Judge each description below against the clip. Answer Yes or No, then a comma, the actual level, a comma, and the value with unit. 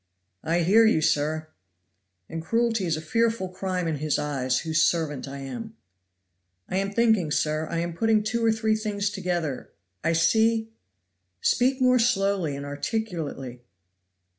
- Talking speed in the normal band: Yes, average, 155 wpm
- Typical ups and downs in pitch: No, wide, 6.3 semitones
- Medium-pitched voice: Yes, medium, 180 Hz